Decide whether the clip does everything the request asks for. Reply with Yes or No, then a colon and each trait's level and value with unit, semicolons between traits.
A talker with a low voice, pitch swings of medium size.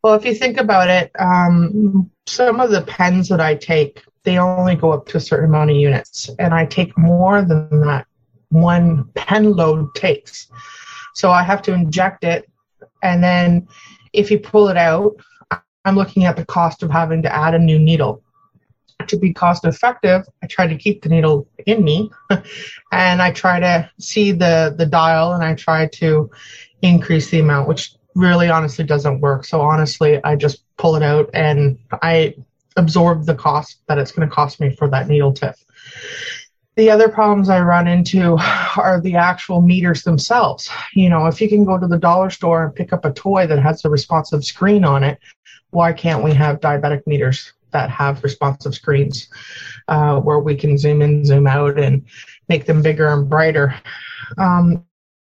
No: medium, 165 Hz; average, 3.6 semitones